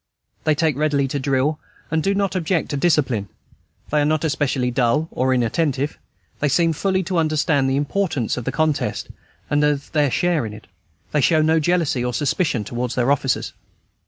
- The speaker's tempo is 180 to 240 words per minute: Yes, average, 185 wpm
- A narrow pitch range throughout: No, average, 3.5 semitones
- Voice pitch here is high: No, medium, 145 Hz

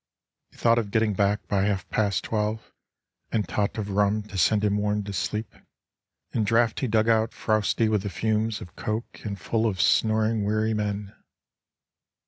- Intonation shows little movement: Yes, narrow, 1.4 semitones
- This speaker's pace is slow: No, average, 170 wpm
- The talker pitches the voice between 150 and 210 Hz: No, low, 105 Hz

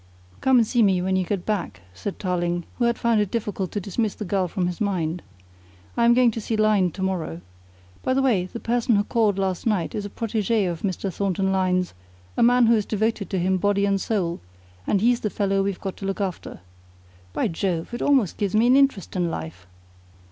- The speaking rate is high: Yes, fast, 220 wpm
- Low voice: No, high, 200 Hz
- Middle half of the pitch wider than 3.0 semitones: Yes, average, 3.4 semitones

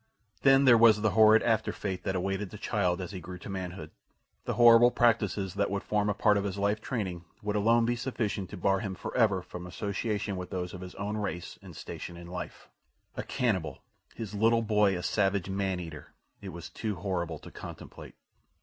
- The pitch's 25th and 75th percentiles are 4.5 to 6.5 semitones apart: No, average, 3.0 semitones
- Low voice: Yes, low, 100 Hz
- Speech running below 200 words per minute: No, fast, 205 wpm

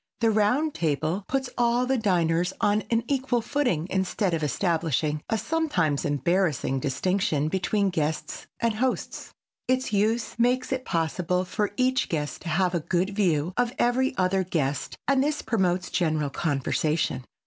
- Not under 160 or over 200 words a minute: No, average, 150 wpm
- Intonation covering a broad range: Yes, wide, 6.9 semitones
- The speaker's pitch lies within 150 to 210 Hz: Yes, high, 190 Hz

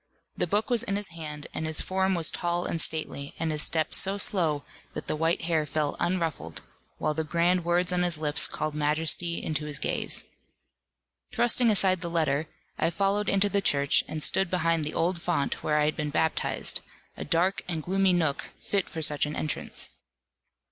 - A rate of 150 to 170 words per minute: No, average, 190 wpm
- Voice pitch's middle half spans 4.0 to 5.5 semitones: No, average, 3.3 semitones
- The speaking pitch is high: No, medium, 165 Hz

